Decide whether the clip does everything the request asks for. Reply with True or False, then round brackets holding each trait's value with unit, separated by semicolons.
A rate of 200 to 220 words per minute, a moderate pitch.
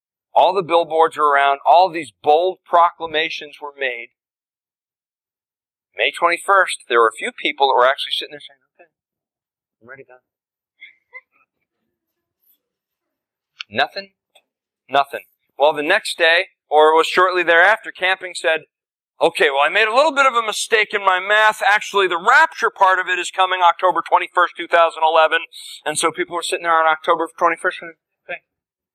False (155 wpm; 170 Hz)